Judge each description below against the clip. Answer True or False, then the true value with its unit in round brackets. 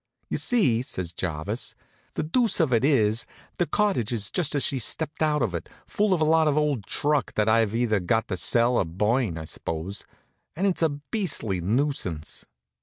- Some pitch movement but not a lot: False (7.3 semitones)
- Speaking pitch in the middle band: False (120 Hz)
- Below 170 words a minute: False (190 wpm)